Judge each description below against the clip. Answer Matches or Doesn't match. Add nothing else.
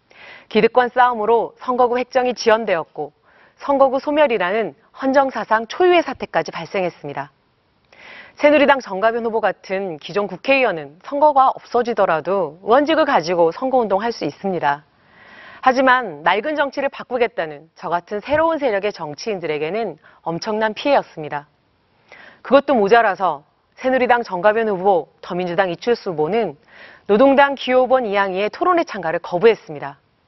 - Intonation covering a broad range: Matches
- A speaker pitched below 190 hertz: Doesn't match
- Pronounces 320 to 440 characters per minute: Matches